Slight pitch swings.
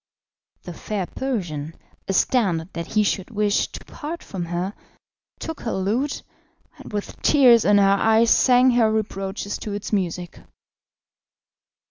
No: average, 3.8 semitones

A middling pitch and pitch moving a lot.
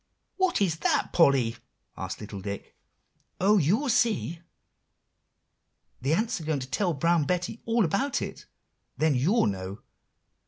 Yes: medium, 165 Hz; wide, 8.4 semitones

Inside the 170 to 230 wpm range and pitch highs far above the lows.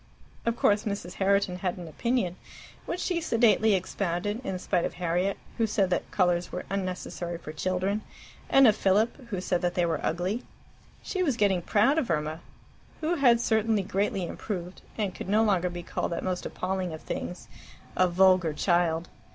No: average, 175 wpm; average, 3.5 semitones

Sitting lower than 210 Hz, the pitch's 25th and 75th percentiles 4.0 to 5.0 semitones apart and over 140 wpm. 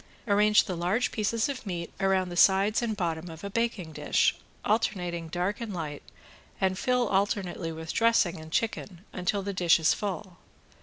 No: high, 190 Hz; average, 3.6 semitones; average, 170 wpm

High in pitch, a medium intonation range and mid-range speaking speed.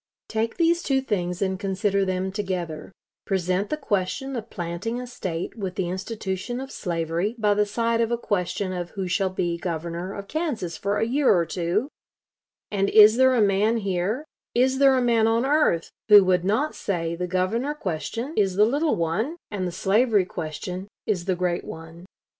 Yes: high, 200 Hz; average, 4.4 semitones; average, 185 wpm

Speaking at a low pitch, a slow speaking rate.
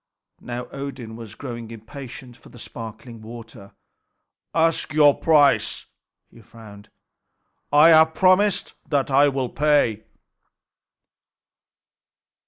Yes: low, 130 Hz; slow, 100 wpm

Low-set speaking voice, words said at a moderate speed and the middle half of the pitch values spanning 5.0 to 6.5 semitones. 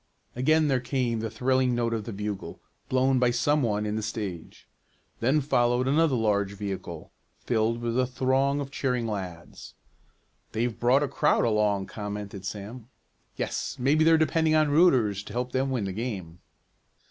No: low, 120 Hz; average, 165 wpm; average, 4.2 semitones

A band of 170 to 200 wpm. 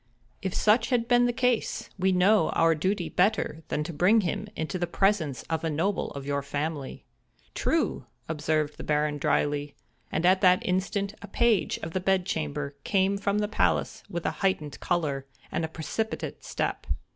Yes: average, 175 wpm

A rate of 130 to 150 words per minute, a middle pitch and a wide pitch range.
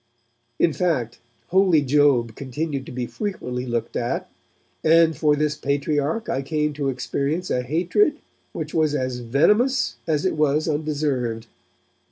No: average, 140 wpm; medium, 150 Hz; average, 3.9 semitones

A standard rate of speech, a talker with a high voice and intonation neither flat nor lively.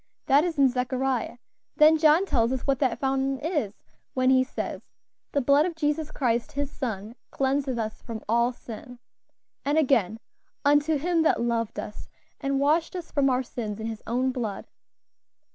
Yes: average, 170 wpm; very high, 265 Hz; average, 3.8 semitones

